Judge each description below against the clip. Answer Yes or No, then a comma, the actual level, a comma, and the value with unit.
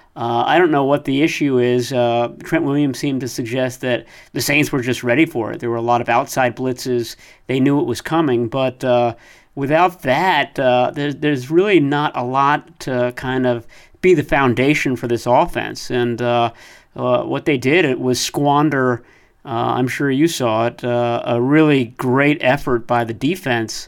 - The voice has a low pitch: Yes, low, 130 Hz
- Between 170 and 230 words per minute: Yes, average, 195 wpm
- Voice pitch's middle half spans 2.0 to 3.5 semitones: Yes, average, 3.0 semitones